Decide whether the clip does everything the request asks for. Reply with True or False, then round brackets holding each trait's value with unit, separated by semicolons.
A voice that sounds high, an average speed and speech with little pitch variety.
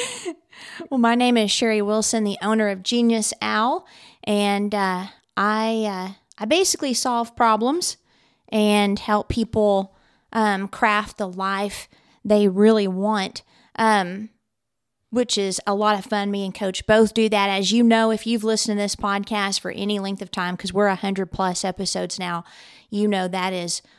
True (205 Hz; 170 wpm; 2.3 semitones)